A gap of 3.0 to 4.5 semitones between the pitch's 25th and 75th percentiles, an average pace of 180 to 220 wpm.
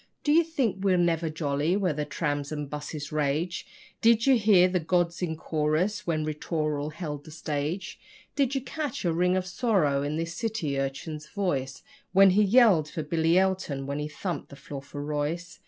Yes: average, 4.2 semitones; average, 190 wpm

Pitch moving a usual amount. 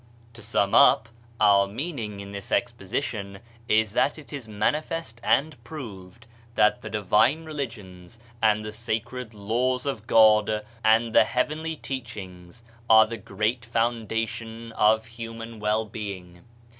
No: narrow, 2.3 semitones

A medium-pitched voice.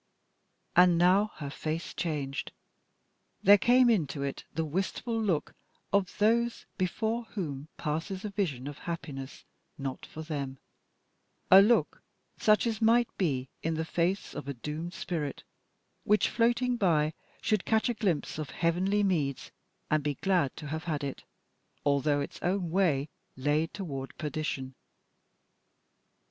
Yes: medium, 170 Hz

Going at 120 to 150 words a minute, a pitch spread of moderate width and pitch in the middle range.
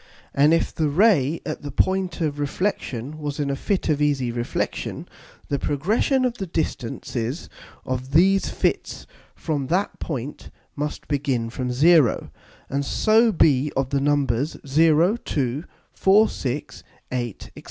Yes: average, 145 wpm; average, 4.2 semitones; medium, 145 Hz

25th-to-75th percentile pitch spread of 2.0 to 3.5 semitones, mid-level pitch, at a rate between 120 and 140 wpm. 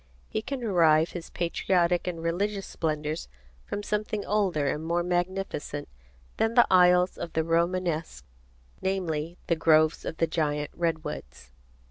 Yes: average, 3.0 semitones; medium, 170 Hz; slow, 135 wpm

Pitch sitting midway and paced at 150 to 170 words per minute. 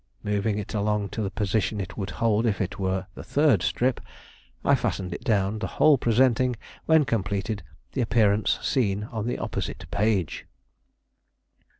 No: low, 105 Hz; average, 160 wpm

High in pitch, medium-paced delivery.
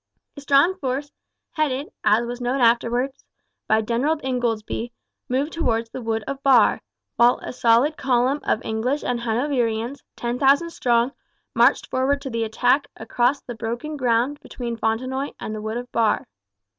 Yes: high, 245 Hz; average, 155 wpm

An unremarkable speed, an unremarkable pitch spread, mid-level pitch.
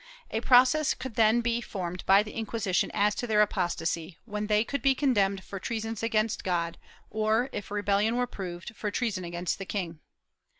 No: average, 180 wpm; average, 3.2 semitones; high, 210 Hz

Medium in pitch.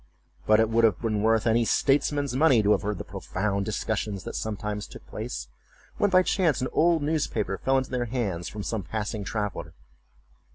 No: low, 110 Hz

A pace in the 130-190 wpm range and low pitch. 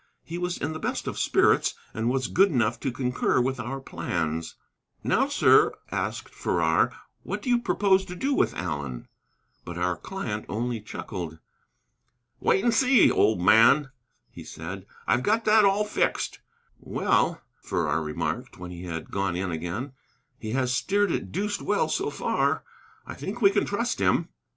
Yes: average, 165 wpm; low, 125 Hz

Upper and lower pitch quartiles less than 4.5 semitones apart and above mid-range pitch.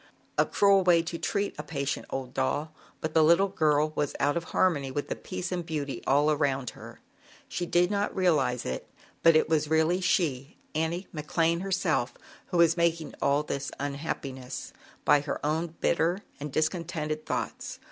No: average, 3.2 semitones; medium, 155 Hz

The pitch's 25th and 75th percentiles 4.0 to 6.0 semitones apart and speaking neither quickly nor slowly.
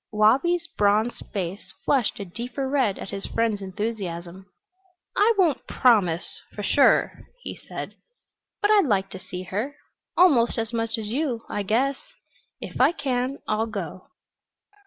Yes: average, 5.1 semitones; average, 145 wpm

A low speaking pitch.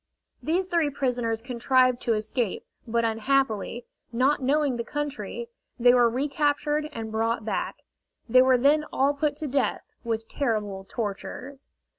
No: very high, 255 Hz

